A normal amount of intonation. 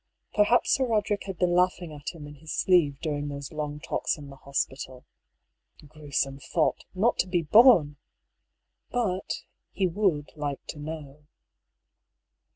Yes: average, 4.2 semitones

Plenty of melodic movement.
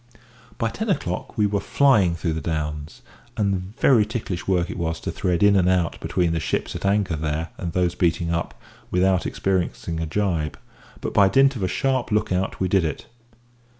No: average, 3.7 semitones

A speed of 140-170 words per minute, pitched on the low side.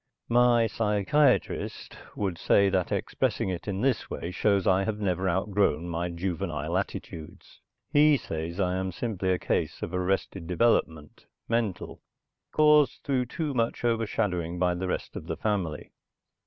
Yes: average, 150 wpm; very low, 95 Hz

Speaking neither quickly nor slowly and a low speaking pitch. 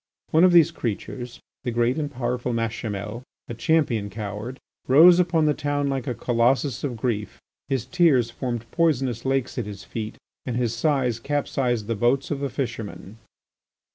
Yes: average, 165 wpm; low, 125 Hz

